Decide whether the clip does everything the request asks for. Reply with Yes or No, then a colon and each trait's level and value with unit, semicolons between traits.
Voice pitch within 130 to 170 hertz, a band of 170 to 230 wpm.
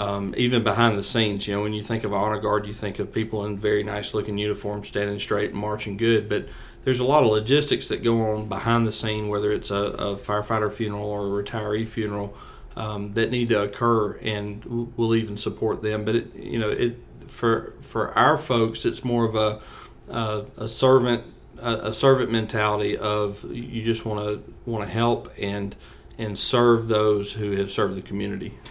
No: low, 105 Hz; average, 200 wpm